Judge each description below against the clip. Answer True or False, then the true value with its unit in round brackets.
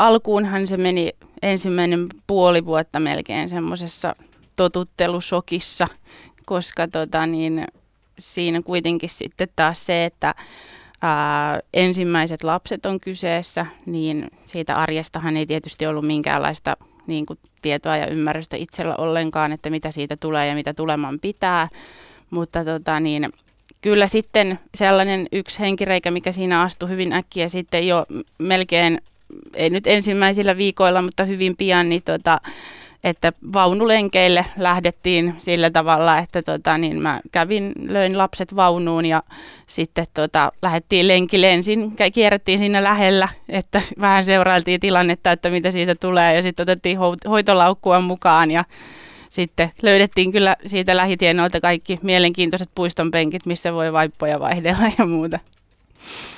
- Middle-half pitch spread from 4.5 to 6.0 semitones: False (2.6 semitones)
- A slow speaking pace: False (125 wpm)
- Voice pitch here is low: False (175 Hz)